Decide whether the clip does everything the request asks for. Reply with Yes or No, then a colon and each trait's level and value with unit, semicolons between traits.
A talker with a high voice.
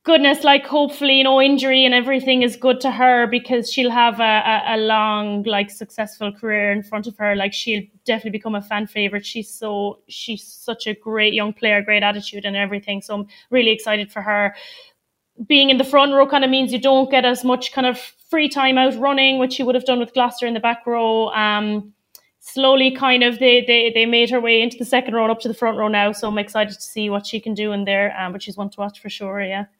Yes: high, 225 Hz